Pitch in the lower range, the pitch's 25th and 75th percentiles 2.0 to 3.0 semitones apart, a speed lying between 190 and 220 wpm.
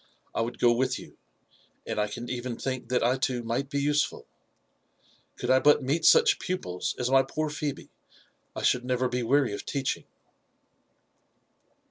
No: low, 130 Hz; average, 2.7 semitones; average, 165 wpm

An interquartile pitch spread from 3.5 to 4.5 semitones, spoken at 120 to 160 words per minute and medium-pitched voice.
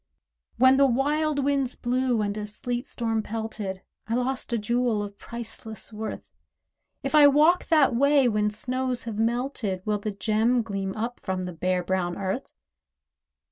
No: average, 3.8 semitones; average, 155 wpm; high, 230 Hz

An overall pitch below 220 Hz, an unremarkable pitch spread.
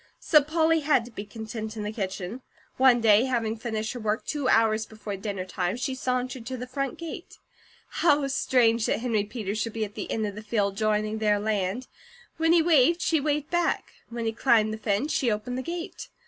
No: high, 230 Hz; average, 3.8 semitones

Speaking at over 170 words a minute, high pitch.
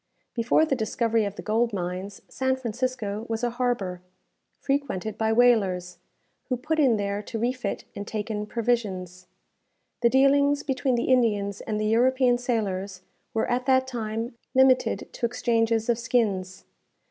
No: average, 150 wpm; high, 230 Hz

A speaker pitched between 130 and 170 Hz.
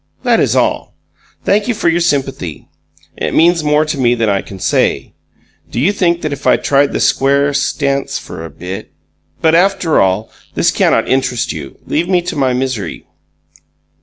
Yes: medium, 140 Hz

